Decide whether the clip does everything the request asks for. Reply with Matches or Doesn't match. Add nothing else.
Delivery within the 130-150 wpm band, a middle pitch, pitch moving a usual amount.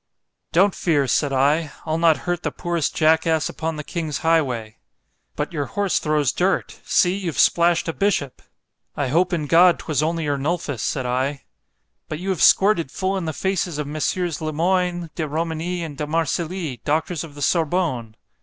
Doesn't match